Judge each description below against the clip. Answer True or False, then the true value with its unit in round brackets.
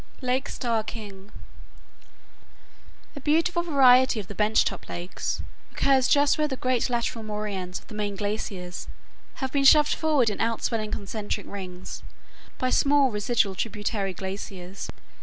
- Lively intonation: False (4.7 semitones)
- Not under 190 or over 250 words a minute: False (140 wpm)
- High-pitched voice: True (220 Hz)